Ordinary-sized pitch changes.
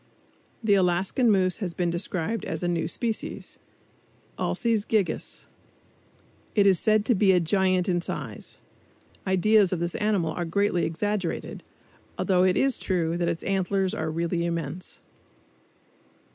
Yes: average, 3.0 semitones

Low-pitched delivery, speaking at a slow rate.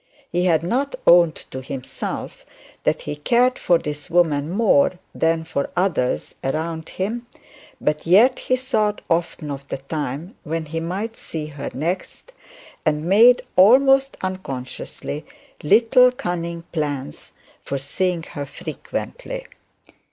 No: medium, 170 Hz; slow, 130 wpm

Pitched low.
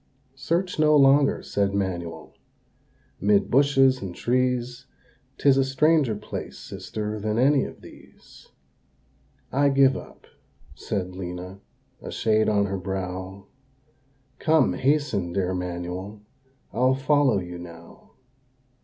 Yes: low, 110 Hz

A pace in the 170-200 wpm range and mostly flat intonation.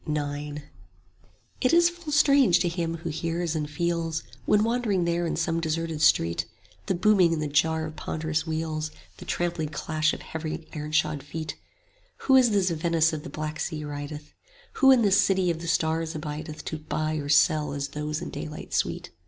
Yes: average, 185 wpm; narrow, 2.2 semitones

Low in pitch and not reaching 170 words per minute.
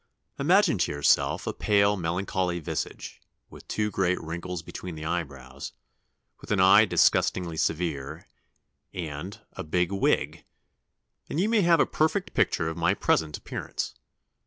Yes: very low, 90 Hz; average, 140 wpm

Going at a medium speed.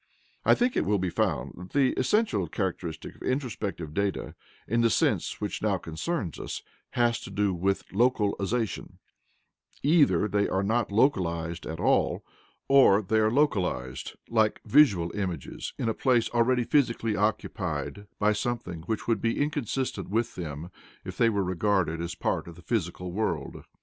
Yes: average, 160 wpm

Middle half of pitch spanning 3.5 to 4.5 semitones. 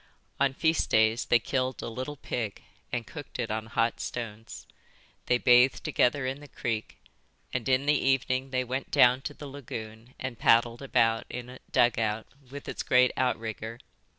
No: narrow, 2.5 semitones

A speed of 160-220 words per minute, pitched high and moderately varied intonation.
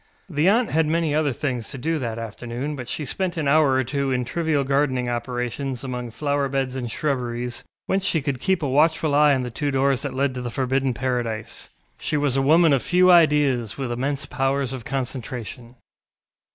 No: average, 200 wpm; low, 135 Hz; average, 3.1 semitones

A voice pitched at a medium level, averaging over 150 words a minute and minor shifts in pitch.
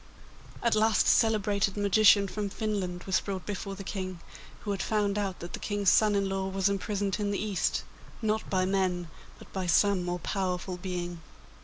No: high, 195 Hz; average, 185 wpm; narrow, 1.9 semitones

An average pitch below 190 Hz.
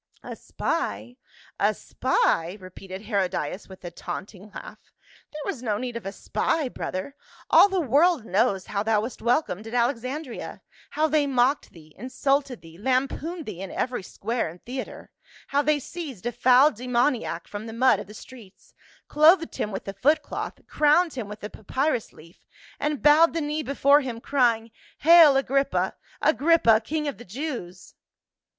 No: very high, 250 Hz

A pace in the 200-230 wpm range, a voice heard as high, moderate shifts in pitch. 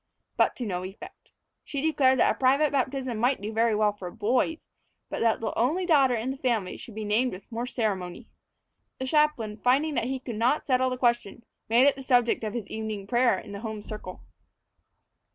Yes: fast, 205 wpm; high, 240 Hz; average, 3.5 semitones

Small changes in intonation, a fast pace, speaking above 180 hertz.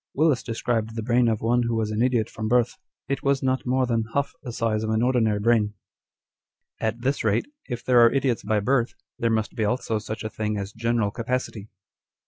No: narrow, 2.2 semitones; fast, 215 wpm; low, 115 Hz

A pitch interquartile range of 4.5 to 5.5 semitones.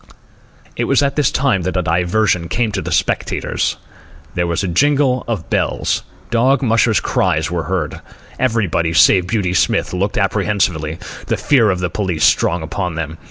Yes: average, 5.2 semitones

